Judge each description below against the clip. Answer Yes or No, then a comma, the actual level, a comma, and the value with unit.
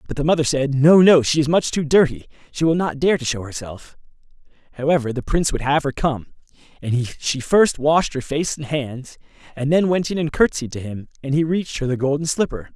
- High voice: No, medium, 145 Hz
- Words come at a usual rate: No, fast, 225 wpm